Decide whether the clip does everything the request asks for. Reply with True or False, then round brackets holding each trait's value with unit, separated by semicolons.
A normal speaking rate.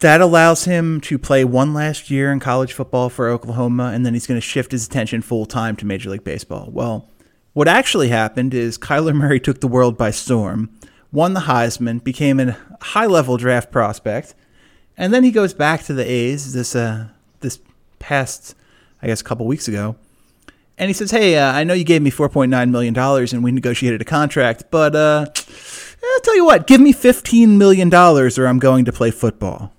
True (195 wpm)